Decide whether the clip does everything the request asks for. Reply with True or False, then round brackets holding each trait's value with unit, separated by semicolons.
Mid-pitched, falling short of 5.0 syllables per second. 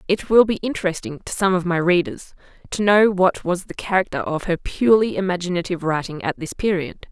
False (180 Hz; 5.8 syllables/s)